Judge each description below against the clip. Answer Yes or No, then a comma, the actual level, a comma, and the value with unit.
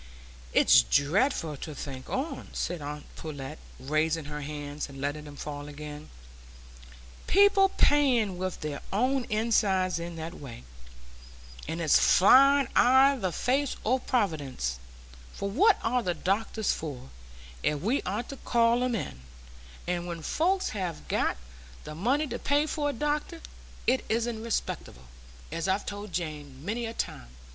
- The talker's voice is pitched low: No, medium, 185 Hz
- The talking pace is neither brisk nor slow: Yes, average, 150 wpm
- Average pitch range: No, wide, 8.9 semitones